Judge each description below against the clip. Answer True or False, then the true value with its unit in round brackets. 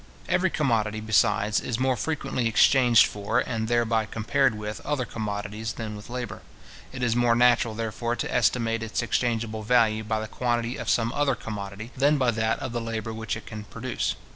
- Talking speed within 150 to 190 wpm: True (185 wpm)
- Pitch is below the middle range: True (115 Hz)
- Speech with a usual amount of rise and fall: False (2.1 semitones)